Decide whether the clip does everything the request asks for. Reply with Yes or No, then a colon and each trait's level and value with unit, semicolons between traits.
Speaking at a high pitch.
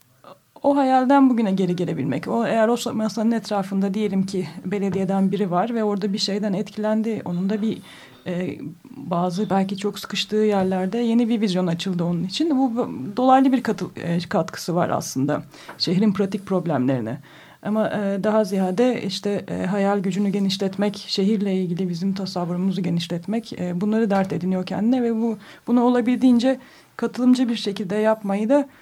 Yes: high, 205 Hz